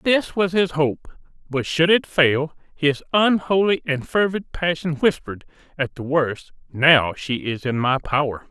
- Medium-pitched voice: Yes, medium, 155 Hz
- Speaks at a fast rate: No, average, 160 wpm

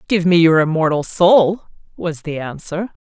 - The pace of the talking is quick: No, average, 160 wpm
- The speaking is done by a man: No, female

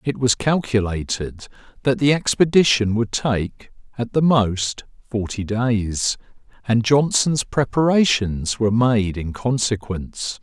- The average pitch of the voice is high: No, low, 115 Hz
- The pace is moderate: No, slow, 115 wpm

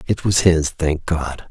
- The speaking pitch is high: No, very low, 85 Hz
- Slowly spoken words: No, average, 200 wpm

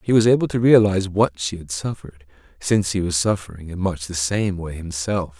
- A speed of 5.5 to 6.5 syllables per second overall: Yes, 5.7 syllables/s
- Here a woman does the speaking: No, male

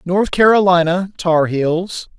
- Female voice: No, male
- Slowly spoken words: Yes, slow, 80 wpm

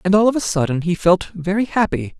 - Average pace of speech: No, fast, 245 wpm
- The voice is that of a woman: No, male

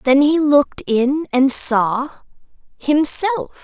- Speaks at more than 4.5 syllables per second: No, 3.6 syllables/s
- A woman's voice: Yes, female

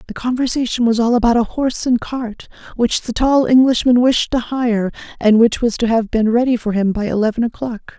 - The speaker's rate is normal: No, fast, 210 wpm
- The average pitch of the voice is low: No, high, 235 Hz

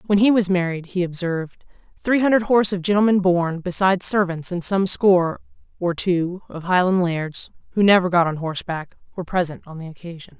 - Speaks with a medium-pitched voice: Yes, medium, 180 Hz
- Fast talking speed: No, average, 180 wpm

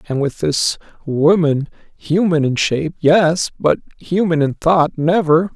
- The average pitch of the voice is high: No, medium, 160 Hz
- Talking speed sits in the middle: No, slow, 110 wpm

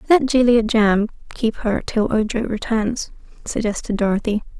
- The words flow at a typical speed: No, slow, 130 wpm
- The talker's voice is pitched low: No, high, 225 Hz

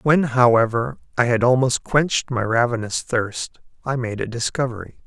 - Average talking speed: Yes, average, 155 wpm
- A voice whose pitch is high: No, low, 120 Hz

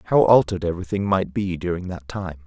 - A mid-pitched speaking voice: No, very low, 90 Hz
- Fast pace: Yes, fast, 220 wpm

